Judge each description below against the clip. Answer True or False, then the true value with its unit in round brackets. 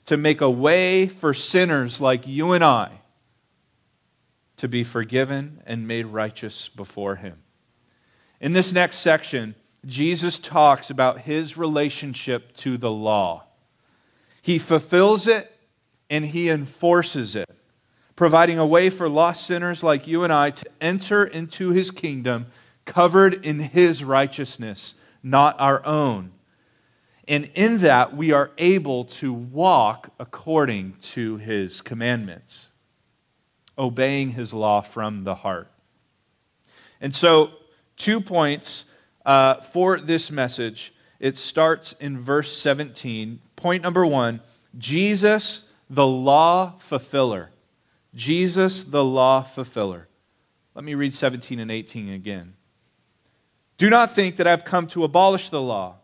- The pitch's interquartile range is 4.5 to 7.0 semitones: True (5.6 semitones)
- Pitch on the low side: False (145 Hz)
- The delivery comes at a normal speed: False (125 wpm)